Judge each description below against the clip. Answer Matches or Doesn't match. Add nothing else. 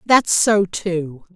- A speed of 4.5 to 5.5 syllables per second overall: Doesn't match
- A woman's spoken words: Matches